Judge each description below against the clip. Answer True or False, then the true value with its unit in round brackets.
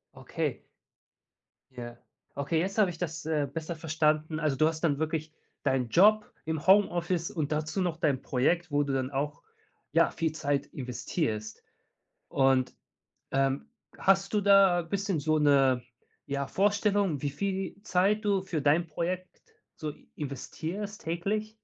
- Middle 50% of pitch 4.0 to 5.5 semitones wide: True (4.8 semitones)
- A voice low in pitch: False (160 Hz)